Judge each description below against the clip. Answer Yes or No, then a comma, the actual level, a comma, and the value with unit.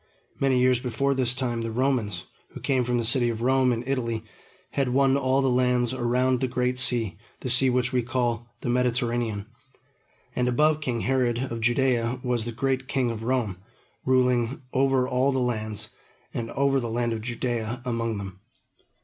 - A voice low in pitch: Yes, low, 125 Hz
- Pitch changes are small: Yes, narrow, 1.9 semitones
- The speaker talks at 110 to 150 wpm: No, average, 180 wpm